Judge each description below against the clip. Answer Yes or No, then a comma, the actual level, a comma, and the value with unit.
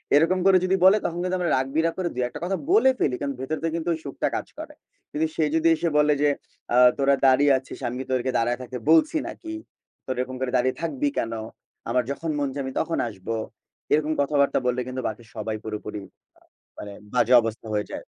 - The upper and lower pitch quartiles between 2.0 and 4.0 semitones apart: No, average, 4.5 semitones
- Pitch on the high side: No, medium, 140 Hz